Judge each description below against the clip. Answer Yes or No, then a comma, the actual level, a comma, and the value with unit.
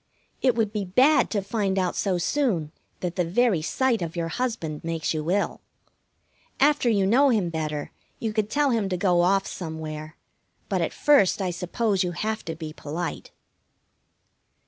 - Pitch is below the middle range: No, high, 190 Hz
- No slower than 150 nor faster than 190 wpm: Yes, average, 170 wpm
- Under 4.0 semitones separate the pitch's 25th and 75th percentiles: No, average, 5.3 semitones